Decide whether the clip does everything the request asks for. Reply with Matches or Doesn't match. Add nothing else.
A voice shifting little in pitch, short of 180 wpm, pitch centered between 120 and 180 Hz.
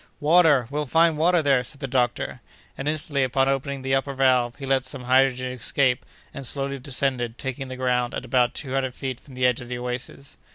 Doesn't match